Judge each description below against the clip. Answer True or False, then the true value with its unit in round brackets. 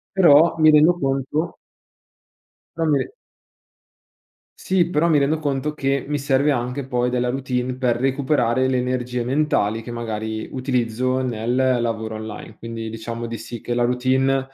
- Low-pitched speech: True (130 Hz)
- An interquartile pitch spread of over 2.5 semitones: True (2.9 semitones)